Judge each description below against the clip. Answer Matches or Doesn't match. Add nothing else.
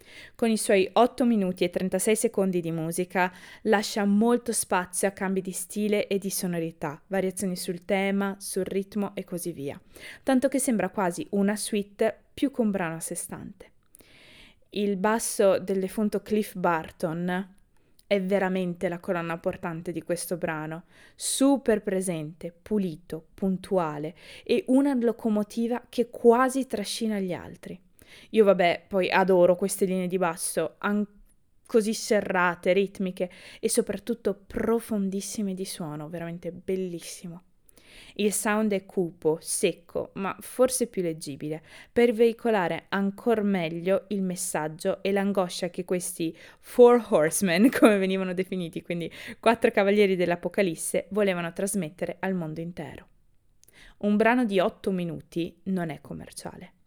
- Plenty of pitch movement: Doesn't match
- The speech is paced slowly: Doesn't match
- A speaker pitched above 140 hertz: Matches